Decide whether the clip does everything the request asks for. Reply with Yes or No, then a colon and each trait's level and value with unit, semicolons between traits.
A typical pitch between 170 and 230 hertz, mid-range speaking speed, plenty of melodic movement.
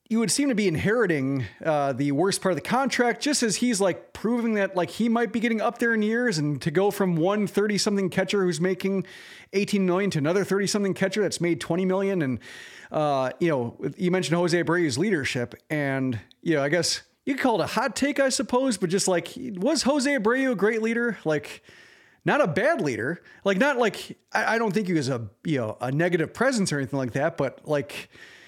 No: high, 190 Hz; fast, 225 wpm; wide, 6.4 semitones